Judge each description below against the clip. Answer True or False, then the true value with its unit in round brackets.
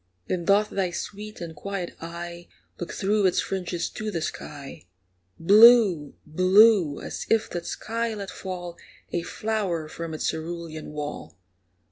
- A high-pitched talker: False (175 Hz)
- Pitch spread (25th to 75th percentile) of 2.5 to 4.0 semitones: True (3.7 semitones)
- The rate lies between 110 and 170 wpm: True (140 wpm)